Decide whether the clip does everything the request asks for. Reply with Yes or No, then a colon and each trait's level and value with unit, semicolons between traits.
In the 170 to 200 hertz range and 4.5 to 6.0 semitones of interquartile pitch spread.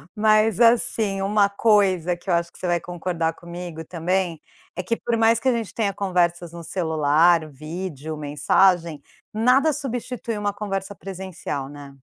No: medium, 185 Hz; average, 4.1 semitones